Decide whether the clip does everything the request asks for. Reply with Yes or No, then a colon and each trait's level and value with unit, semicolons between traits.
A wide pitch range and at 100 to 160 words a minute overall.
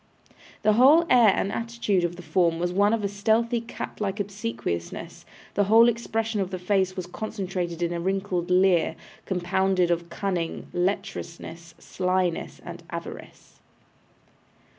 No: average, 3.2 semitones; average, 140 wpm